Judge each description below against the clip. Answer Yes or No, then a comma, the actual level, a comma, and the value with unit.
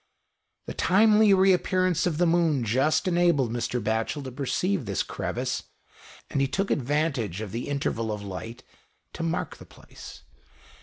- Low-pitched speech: No, medium, 145 Hz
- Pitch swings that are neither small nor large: No, wide, 7.2 semitones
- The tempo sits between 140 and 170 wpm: Yes, average, 155 wpm